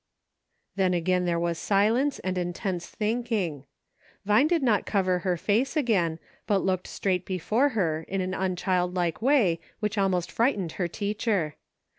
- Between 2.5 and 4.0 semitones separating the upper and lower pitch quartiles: Yes, average, 3.5 semitones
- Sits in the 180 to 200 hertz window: Yes, high, 190 Hz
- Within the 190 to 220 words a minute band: No, average, 160 wpm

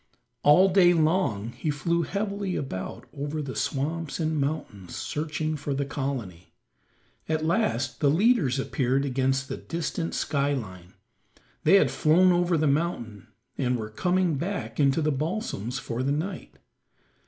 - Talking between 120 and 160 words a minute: Yes, average, 145 wpm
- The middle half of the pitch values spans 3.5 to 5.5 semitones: Yes, average, 4.2 semitones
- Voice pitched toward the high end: No, medium, 150 Hz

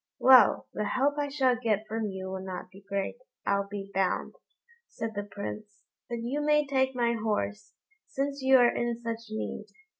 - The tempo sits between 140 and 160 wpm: No, average, 180 wpm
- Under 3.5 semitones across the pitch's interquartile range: No, average, 4.6 semitones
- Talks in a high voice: Yes, high, 225 Hz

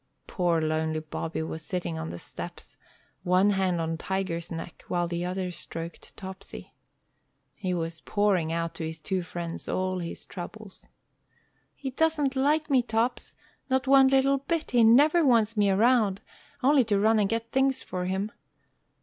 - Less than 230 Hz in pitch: Yes, high, 190 Hz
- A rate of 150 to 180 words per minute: Yes, average, 160 wpm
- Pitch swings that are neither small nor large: No, wide, 6.4 semitones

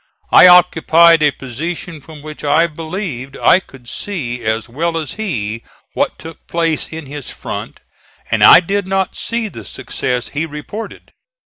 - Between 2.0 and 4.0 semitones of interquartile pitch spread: No, average, 4.7 semitones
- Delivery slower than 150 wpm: No, average, 155 wpm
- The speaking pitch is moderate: Yes, medium, 160 Hz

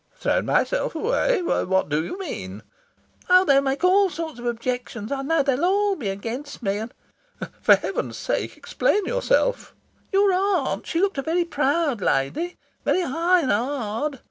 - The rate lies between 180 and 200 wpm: No, average, 170 wpm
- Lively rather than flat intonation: Yes, wide, 7.4 semitones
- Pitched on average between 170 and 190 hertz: No, very high, 295 Hz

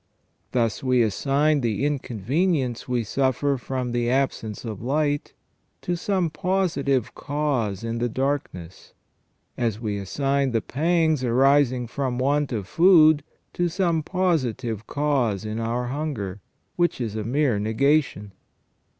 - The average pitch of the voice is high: No, low, 130 Hz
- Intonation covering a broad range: No, average, 4.4 semitones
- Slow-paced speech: Yes, slow, 130 wpm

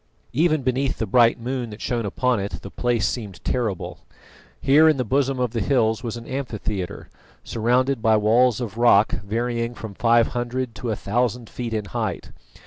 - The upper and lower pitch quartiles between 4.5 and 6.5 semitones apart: No, narrow, 2.4 semitones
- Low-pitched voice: Yes, low, 120 Hz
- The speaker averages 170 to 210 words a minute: Yes, average, 180 wpm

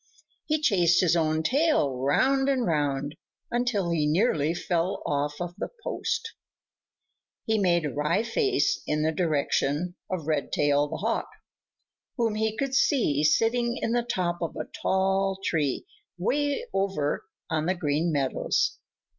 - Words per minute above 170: No, average, 145 wpm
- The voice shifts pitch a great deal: Yes, wide, 7.3 semitones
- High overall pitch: No, medium, 175 Hz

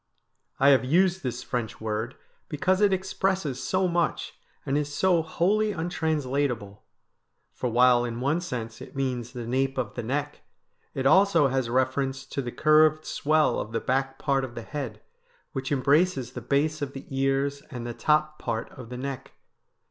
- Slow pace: No, average, 170 wpm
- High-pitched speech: No, low, 135 Hz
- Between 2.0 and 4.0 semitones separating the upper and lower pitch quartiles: Yes, average, 3.7 semitones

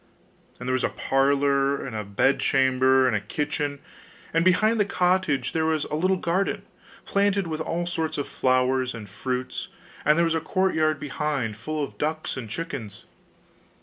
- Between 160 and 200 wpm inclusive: Yes, average, 170 wpm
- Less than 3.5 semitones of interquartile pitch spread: No, average, 4.2 semitones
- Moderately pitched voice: Yes, medium, 145 Hz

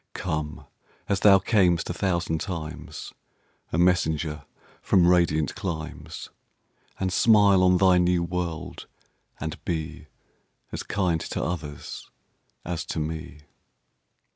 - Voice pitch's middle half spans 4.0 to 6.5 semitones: No, narrow, 2.5 semitones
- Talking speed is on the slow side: Yes, slow, 100 wpm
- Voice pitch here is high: No, very low, 85 Hz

